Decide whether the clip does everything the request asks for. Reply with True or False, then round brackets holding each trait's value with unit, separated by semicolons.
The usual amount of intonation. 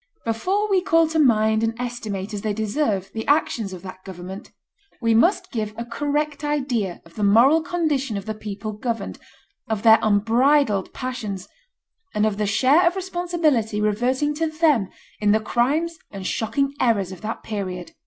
False (6.0 semitones)